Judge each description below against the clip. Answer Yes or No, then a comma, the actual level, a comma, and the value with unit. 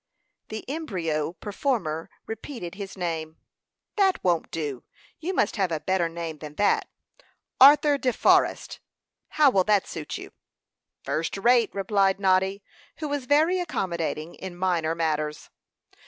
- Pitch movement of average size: No, wide, 7.2 semitones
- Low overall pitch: No, high, 190 Hz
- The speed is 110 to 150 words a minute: Yes, slow, 135 wpm